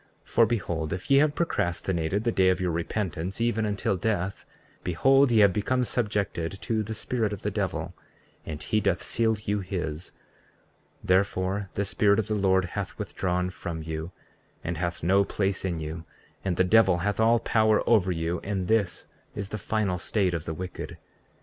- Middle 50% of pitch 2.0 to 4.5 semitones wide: Yes, average, 3.5 semitones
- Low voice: Yes, very low, 95 Hz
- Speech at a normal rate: Yes, average, 180 wpm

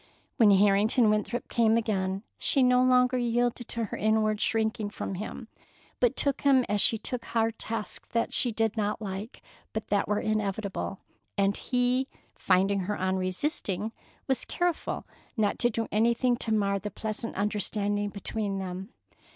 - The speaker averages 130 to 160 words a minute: Yes, average, 155 wpm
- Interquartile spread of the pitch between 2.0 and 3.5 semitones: Yes, average, 2.9 semitones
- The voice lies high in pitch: Yes, high, 215 Hz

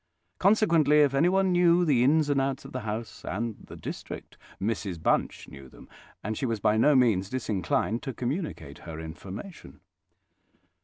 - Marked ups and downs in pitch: Yes, wide, 6.2 semitones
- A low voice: Yes, low, 125 Hz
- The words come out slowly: No, average, 160 wpm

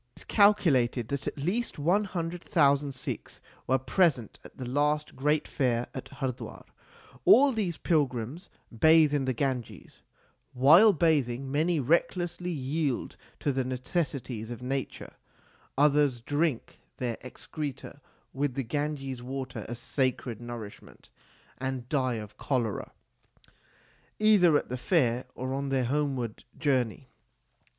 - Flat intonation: No, average, 3.7 semitones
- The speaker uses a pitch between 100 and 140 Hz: Yes, low, 135 Hz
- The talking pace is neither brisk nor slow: No, slow, 130 wpm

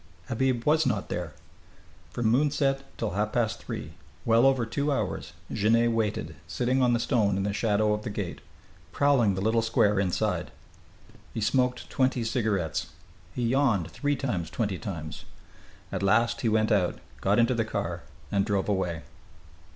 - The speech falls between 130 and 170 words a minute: Yes, average, 160 wpm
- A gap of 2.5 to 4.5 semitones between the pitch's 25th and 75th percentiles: Yes, average, 3.7 semitones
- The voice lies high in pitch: No, low, 110 Hz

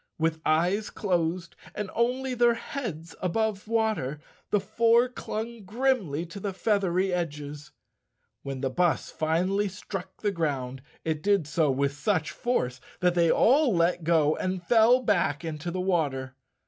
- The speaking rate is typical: Yes, average, 150 wpm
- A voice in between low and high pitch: Yes, medium, 180 Hz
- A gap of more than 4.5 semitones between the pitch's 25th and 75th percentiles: Yes, wide, 5.4 semitones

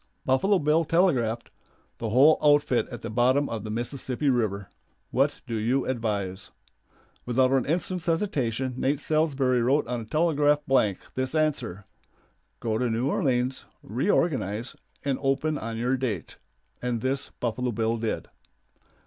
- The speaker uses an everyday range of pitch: Yes, average, 4.0 semitones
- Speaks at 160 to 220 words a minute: No, average, 140 wpm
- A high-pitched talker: No, low, 130 Hz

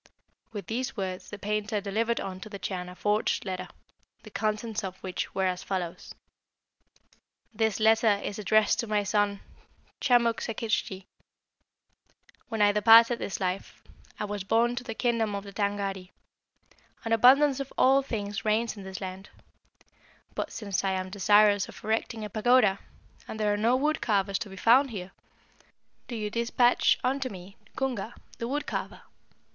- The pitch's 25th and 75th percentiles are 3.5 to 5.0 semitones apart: No, average, 2.9 semitones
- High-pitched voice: Yes, high, 210 Hz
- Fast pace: No, average, 160 wpm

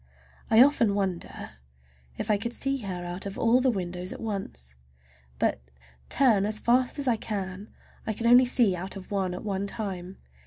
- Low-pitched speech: No, high, 205 Hz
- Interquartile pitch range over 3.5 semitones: Yes, average, 4.0 semitones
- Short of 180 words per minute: No, average, 185 wpm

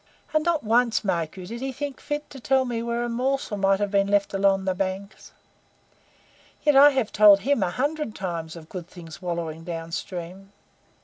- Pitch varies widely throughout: Yes, wide, 5.9 semitones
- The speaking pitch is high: Yes, high, 200 Hz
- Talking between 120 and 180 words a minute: No, average, 195 wpm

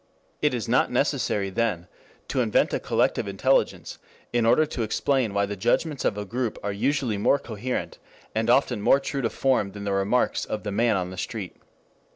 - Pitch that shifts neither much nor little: Yes, average, 4.1 semitones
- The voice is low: Yes, low, 110 Hz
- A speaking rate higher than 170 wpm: Yes, average, 190 wpm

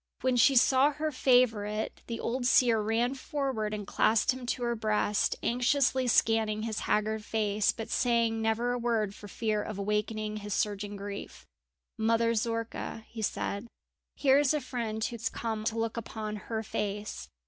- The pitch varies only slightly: Yes, narrow, 2.3 semitones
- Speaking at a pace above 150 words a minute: Yes, average, 170 wpm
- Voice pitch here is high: Yes, high, 225 Hz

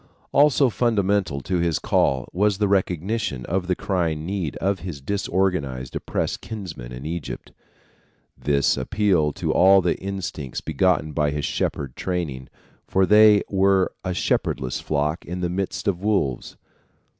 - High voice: No, very low, 90 Hz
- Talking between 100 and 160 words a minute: Yes, average, 145 wpm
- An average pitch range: Yes, average, 4.7 semitones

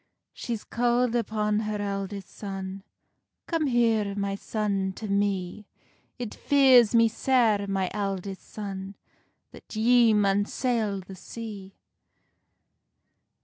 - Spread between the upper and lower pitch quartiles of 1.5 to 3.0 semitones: Yes, average, 2.7 semitones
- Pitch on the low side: No, high, 210 Hz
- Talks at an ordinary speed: No, slow, 110 wpm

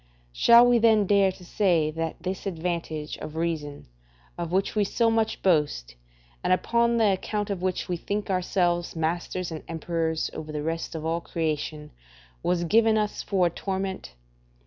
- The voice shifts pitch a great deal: No, average, 3.8 semitones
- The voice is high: No, medium, 175 Hz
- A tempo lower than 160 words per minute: No, average, 170 wpm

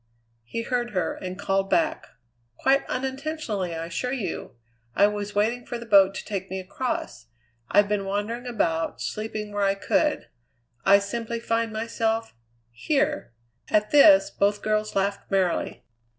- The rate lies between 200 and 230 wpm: No, average, 150 wpm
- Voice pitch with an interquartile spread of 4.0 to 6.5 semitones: No, average, 3.5 semitones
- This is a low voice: No, high, 210 Hz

